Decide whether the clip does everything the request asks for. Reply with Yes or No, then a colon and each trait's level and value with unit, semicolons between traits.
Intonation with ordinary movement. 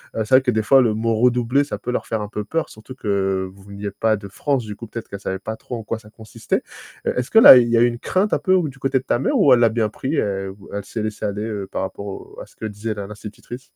Yes: average, 3.4 semitones